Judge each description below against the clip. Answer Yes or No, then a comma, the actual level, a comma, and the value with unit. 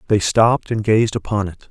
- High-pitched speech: No, low, 105 Hz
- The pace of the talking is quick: Yes, fast, 210 wpm